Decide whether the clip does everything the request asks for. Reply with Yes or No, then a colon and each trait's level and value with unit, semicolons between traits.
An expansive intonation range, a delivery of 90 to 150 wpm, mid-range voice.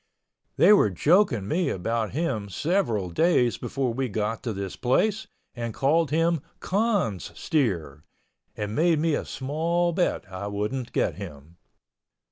No: wide, 8.2 semitones; average, 140 wpm; low, 130 Hz